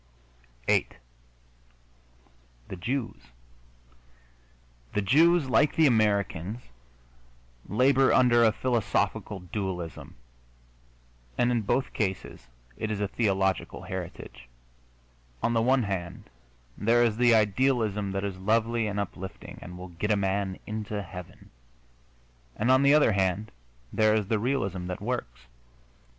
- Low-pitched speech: Yes, low, 105 Hz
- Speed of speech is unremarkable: No, slow, 120 wpm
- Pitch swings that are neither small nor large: Yes, average, 3.9 semitones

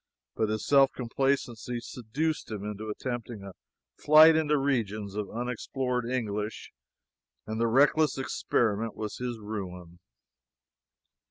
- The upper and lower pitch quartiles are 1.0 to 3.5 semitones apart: No, average, 3.9 semitones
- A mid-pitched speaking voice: No, low, 115 Hz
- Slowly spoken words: Yes, slow, 115 wpm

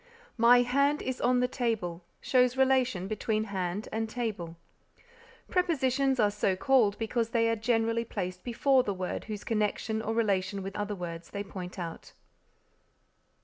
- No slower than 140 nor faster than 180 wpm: Yes, average, 150 wpm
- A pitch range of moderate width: Yes, average, 4.0 semitones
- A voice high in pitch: Yes, high, 220 Hz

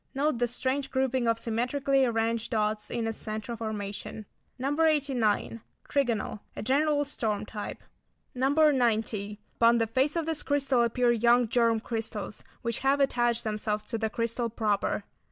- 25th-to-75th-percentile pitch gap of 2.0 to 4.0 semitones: Yes, average, 3.4 semitones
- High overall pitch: Yes, high, 235 Hz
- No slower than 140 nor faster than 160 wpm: Yes, average, 155 wpm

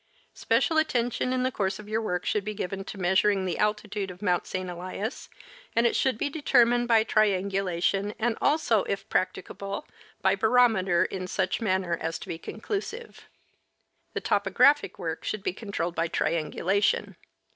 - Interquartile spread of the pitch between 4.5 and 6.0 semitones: No, average, 3.9 semitones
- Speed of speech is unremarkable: Yes, average, 160 wpm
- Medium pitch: No, high, 200 Hz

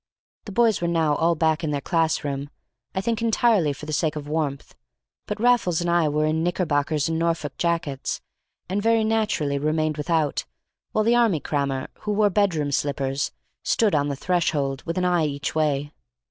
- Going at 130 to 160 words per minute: No, average, 185 wpm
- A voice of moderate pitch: Yes, medium, 160 Hz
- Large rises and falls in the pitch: No, average, 3.9 semitones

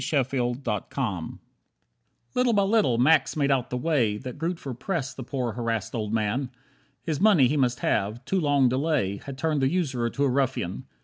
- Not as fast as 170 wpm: No, average, 175 wpm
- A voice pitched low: Yes, low, 130 Hz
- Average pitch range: Yes, average, 4.1 semitones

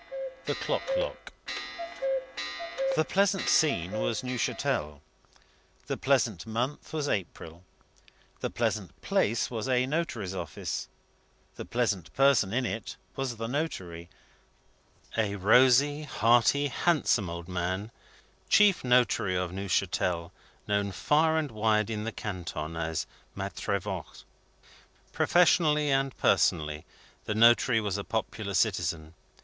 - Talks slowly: Yes, slow, 115 wpm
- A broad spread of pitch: Yes, wide, 6.5 semitones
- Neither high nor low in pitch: No, low, 110 Hz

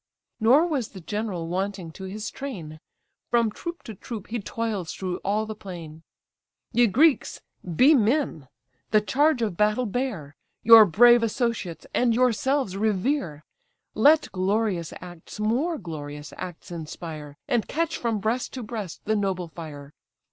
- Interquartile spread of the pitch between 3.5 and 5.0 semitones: No, wide, 5.5 semitones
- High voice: Yes, high, 210 Hz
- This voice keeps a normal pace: Yes, average, 145 wpm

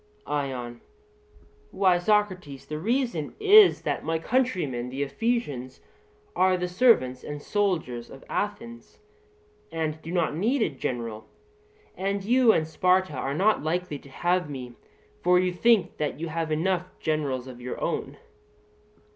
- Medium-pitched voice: Yes, medium, 165 Hz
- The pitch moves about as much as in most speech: No, wide, 6.1 semitones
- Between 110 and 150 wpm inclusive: Yes, average, 140 wpm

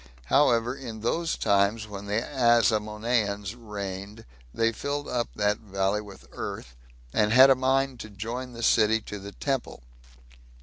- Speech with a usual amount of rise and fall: Yes, average, 3.2 semitones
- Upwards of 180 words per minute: No, average, 145 wpm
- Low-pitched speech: Yes, low, 110 Hz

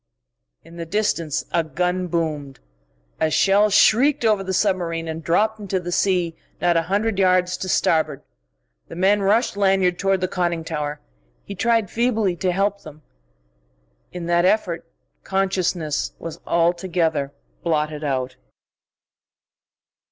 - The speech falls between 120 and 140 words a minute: Yes, slow, 135 wpm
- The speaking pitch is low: No, medium, 180 Hz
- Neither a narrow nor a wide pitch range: Yes, average, 3.1 semitones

